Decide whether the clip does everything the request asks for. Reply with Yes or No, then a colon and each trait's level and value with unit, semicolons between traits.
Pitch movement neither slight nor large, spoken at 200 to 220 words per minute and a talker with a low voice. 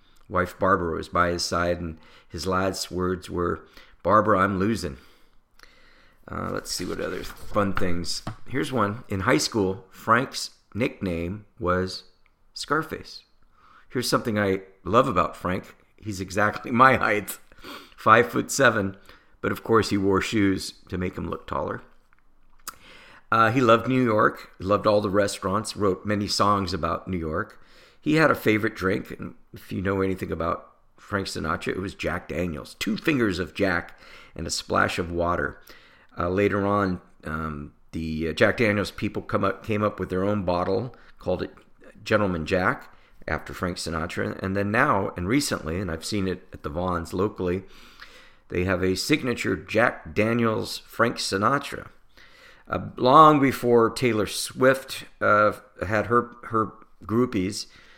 No: average, 3.0 semitones; average, 155 wpm; very low, 95 Hz